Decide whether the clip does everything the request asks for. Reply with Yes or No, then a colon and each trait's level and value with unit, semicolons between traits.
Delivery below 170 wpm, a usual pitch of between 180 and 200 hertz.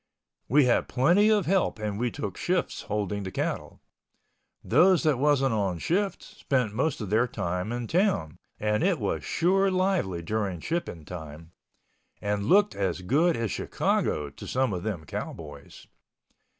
No: average, 150 wpm; low, 115 Hz